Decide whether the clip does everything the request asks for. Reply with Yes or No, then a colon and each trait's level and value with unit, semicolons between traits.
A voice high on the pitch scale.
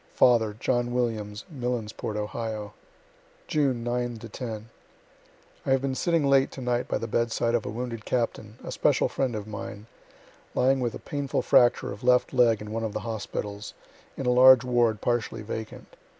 No: low, 120 Hz